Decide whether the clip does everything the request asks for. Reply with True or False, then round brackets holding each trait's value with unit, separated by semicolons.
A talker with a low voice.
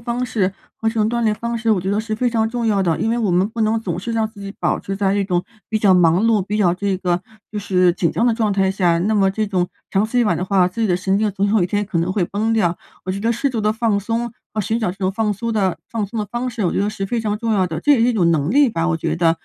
False (205 Hz)